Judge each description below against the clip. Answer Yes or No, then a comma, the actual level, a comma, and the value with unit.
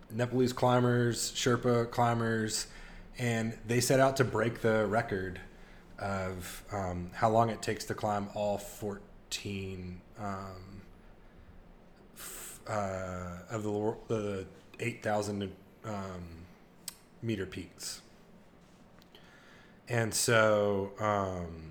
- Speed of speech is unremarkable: No, slow, 90 wpm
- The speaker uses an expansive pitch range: No, average, 3.2 semitones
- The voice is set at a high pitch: No, low, 105 Hz